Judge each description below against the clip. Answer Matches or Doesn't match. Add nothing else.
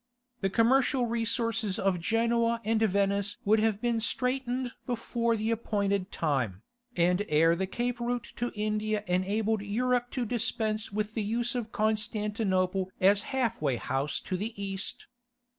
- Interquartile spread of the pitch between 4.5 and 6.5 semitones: Doesn't match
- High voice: Matches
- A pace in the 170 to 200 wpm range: Doesn't match